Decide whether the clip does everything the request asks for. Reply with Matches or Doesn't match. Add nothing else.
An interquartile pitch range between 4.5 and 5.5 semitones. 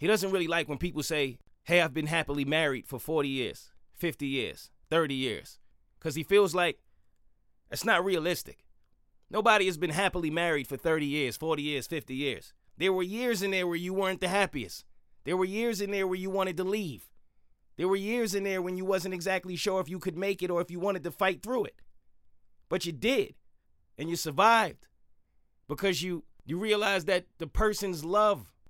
Matches